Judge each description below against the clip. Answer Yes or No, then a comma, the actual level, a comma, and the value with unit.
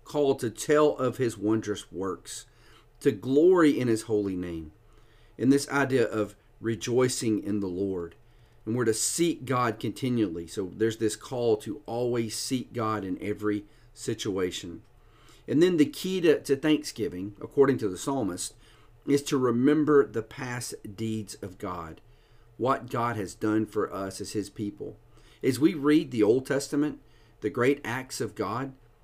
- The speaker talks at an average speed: Yes, average, 160 wpm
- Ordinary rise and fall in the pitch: Yes, average, 4.2 semitones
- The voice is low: Yes, low, 115 Hz